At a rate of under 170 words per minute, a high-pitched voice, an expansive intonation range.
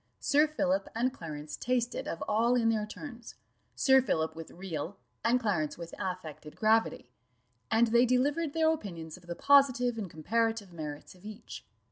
Yes: average, 160 wpm; high, 220 Hz; wide, 6.7 semitones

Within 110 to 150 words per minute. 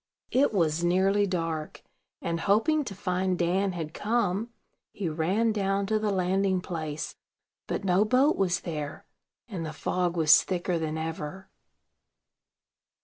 Yes: average, 140 wpm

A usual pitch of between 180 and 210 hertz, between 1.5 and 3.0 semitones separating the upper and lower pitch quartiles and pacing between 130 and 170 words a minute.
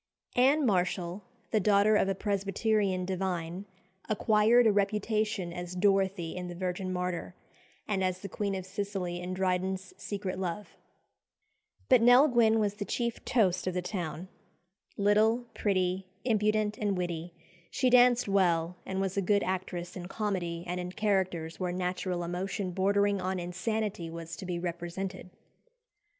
Yes: high, 190 Hz; narrow, 2.6 semitones; average, 150 wpm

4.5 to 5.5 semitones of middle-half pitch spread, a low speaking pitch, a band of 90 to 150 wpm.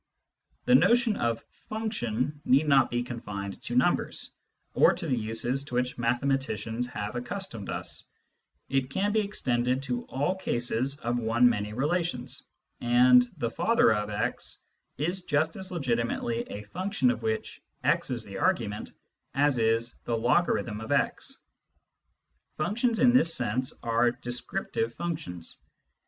Yes: average, 4.9 semitones; low, 125 Hz; average, 145 wpm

